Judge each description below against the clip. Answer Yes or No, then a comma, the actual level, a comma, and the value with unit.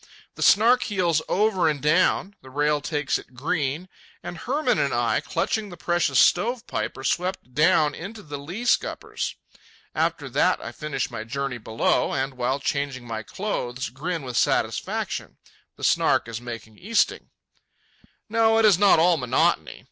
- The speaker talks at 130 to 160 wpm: Yes, average, 155 wpm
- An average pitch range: No, wide, 6.6 semitones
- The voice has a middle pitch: Yes, medium, 150 Hz